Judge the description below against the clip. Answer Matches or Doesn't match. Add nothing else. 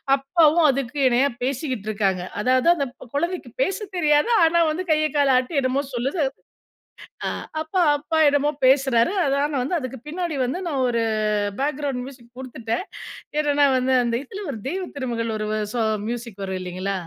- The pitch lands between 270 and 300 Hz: Matches